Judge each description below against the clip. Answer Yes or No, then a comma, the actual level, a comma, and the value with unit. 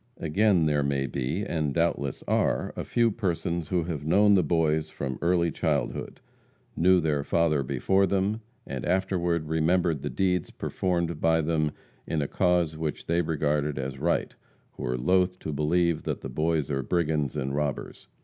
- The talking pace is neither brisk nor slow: Yes, average, 170 wpm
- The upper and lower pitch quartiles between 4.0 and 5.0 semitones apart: No, average, 3.2 semitones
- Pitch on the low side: Yes, very low, 80 Hz